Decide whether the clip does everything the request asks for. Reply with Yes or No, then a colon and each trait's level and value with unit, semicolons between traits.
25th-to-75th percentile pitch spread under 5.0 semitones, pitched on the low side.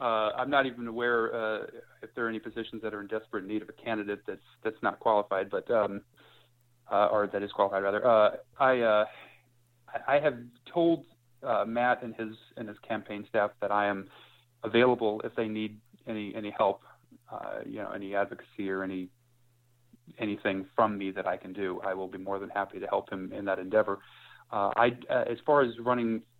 Yes: average, 2.9 semitones; low, 110 Hz